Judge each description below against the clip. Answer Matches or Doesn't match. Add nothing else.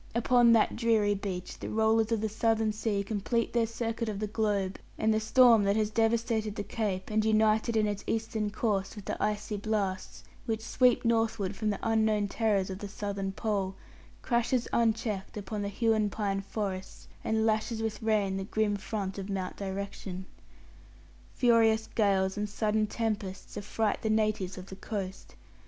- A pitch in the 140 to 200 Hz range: Doesn't match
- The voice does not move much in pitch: Matches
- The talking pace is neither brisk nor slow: Matches